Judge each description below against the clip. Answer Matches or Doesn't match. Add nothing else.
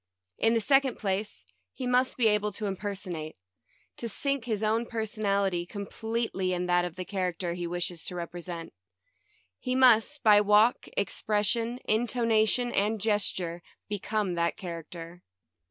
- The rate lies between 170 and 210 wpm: Doesn't match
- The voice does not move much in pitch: Doesn't match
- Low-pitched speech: Doesn't match